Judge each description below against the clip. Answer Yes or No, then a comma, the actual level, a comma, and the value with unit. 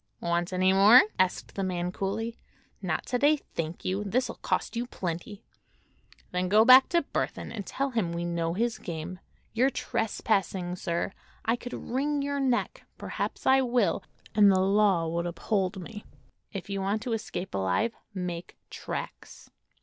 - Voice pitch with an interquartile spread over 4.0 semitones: Yes, average, 4.8 semitones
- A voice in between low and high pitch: No, high, 195 Hz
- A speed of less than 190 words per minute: Yes, average, 155 wpm